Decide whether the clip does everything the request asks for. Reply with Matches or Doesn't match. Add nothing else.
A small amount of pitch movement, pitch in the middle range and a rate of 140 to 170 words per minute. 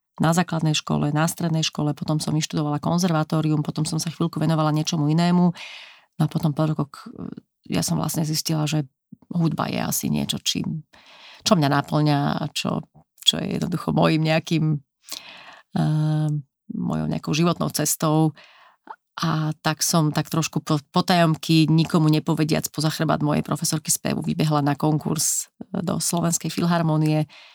Matches